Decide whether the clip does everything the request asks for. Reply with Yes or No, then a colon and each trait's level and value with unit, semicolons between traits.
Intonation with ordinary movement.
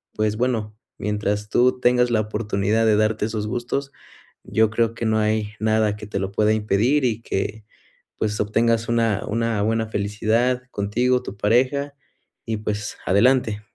No: narrow, 2.0 semitones